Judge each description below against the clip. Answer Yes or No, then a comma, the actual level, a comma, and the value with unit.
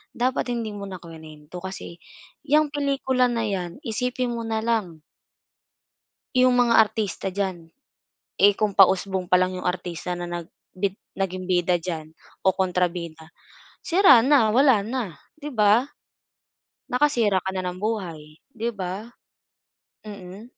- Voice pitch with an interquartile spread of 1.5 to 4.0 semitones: No, average, 4.9 semitones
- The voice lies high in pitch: Yes, high, 200 Hz